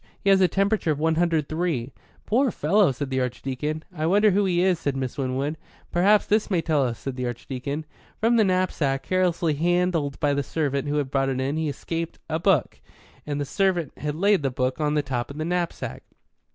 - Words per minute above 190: Yes, fast, 205 wpm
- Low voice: No, medium, 155 Hz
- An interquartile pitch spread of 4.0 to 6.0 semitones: Yes, average, 4.7 semitones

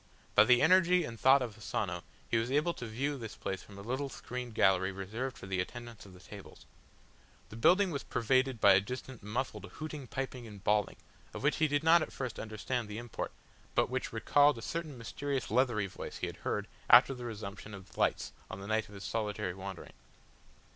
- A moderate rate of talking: No, fast, 210 wpm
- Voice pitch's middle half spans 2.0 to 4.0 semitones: No, average, 4.5 semitones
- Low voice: Yes, low, 115 Hz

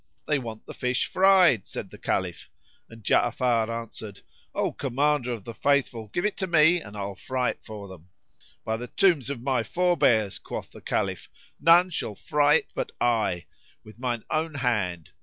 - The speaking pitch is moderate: No, low, 125 Hz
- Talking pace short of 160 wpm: No, average, 175 wpm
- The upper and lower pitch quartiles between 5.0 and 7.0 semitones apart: Yes, wide, 5.4 semitones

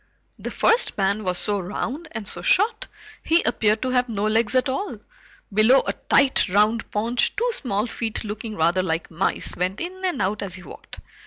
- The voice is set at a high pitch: Yes, high, 220 Hz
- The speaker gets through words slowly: No, average, 190 wpm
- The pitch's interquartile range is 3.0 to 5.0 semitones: Yes, average, 4.6 semitones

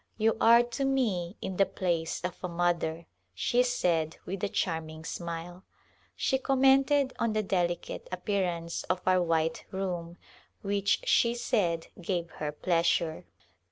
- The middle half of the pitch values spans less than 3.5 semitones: No, average, 4.3 semitones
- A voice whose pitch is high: No, medium, 180 Hz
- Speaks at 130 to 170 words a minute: Yes, average, 155 wpm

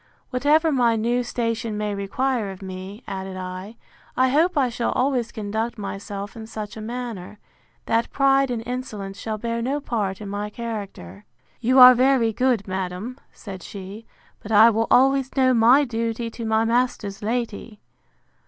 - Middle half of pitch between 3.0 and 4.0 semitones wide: Yes, average, 3.6 semitones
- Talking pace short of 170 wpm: Yes, average, 160 wpm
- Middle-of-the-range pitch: No, high, 225 Hz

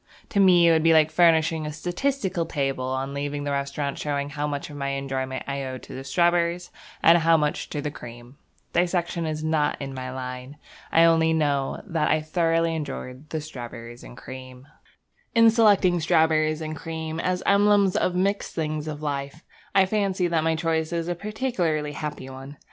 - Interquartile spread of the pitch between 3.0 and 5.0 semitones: Yes, average, 3.6 semitones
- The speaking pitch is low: No, medium, 155 Hz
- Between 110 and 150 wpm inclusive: No, average, 180 wpm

